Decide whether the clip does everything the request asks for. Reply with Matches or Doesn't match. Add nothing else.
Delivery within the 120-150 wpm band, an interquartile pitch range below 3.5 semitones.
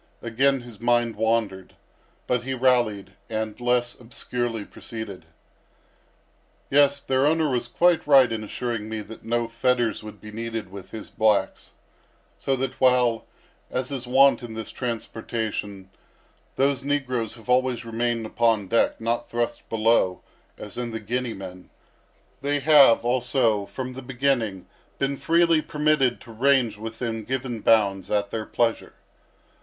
Matches